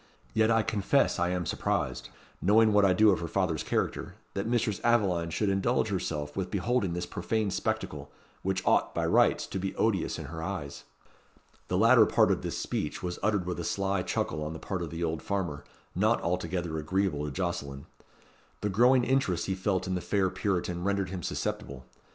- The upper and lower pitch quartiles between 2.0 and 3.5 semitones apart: Yes, average, 3.2 semitones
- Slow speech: No, average, 190 wpm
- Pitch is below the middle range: Yes, very low, 95 Hz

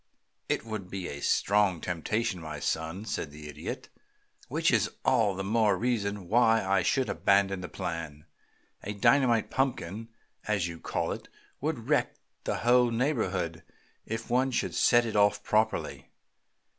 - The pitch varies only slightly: No, average, 4.3 semitones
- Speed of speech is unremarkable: Yes, average, 150 wpm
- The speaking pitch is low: Yes, low, 100 Hz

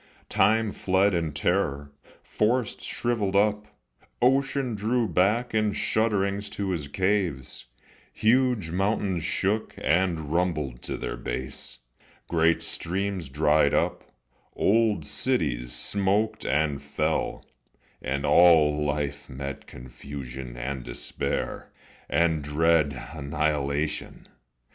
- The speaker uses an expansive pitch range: Yes, wide, 6.2 semitones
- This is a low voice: Yes, very low, 85 Hz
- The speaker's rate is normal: No, slow, 100 wpm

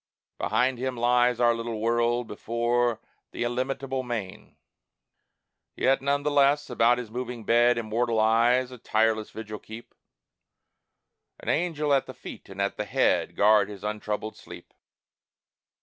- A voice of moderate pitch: No, low, 120 Hz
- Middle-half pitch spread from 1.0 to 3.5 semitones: Yes, narrow, 2.4 semitones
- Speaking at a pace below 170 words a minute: Yes, average, 140 wpm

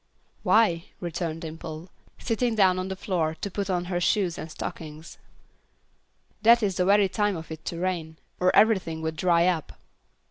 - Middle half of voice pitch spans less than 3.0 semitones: No, average, 3.3 semitones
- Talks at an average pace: Yes, average, 170 wpm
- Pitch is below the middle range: No, medium, 180 Hz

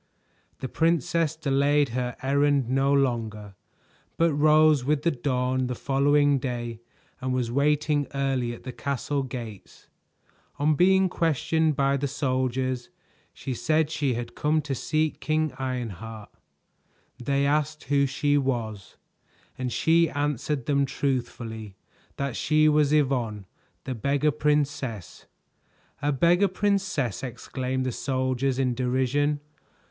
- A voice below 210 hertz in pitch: Yes, medium, 140 Hz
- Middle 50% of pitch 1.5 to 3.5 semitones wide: Yes, average, 2.8 semitones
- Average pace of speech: No, slow, 125 wpm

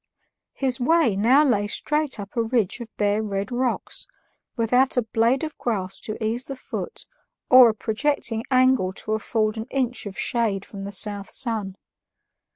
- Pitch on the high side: Yes, high, 230 Hz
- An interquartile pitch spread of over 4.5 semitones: No, average, 3.7 semitones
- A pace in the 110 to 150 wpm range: No, average, 165 wpm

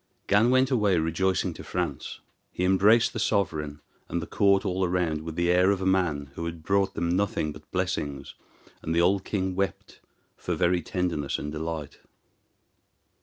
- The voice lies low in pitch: Yes, very low, 90 Hz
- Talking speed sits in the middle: Yes, average, 170 wpm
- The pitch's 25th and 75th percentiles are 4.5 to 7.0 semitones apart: No, average, 3.2 semitones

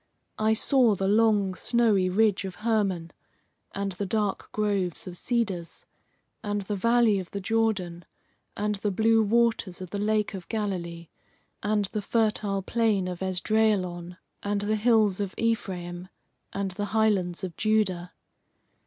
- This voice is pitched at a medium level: No, high, 205 Hz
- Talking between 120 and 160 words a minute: Yes, average, 145 wpm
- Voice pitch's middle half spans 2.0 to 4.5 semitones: Yes, average, 2.8 semitones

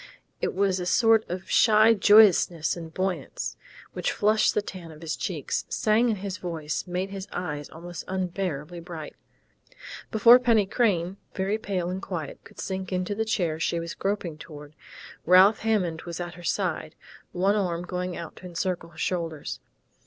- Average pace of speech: Yes, average, 165 wpm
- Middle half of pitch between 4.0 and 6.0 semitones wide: No, average, 3.1 semitones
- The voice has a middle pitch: Yes, medium, 180 Hz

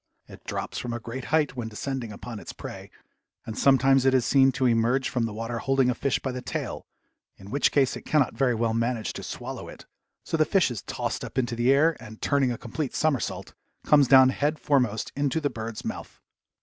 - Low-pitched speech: Yes, low, 130 Hz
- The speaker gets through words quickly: Yes, fast, 215 wpm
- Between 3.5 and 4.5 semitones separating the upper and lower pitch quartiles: No, average, 3.1 semitones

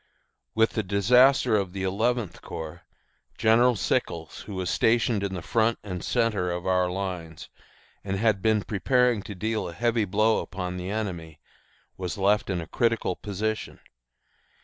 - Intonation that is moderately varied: Yes, average, 3.6 semitones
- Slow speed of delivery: No, average, 155 wpm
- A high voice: No, low, 100 Hz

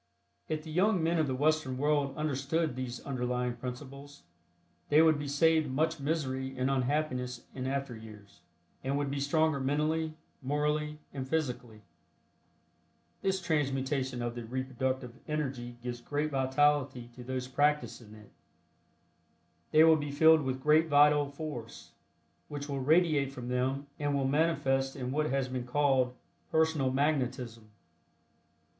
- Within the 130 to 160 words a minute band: Yes, average, 140 wpm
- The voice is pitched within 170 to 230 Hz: No, medium, 140 Hz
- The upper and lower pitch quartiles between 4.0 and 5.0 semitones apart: No, average, 3.0 semitones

